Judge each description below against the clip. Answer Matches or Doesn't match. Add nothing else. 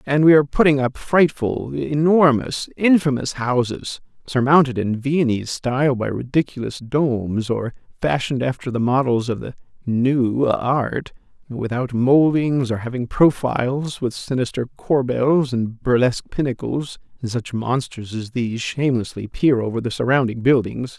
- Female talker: Doesn't match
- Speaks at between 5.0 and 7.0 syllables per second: Doesn't match